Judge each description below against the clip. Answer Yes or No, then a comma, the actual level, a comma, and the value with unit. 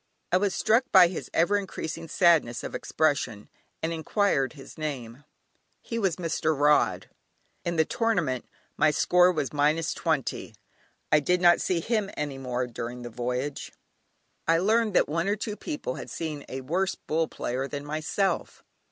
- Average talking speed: Yes, average, 160 wpm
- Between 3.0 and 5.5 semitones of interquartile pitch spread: Yes, average, 4.6 semitones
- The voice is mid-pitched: Yes, medium, 160 Hz